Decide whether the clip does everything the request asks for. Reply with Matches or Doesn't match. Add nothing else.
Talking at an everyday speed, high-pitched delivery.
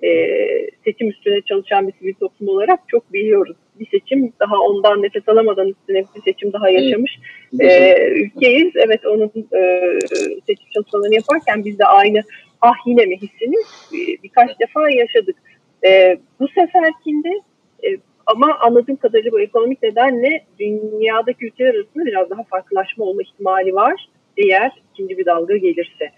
Doesn't match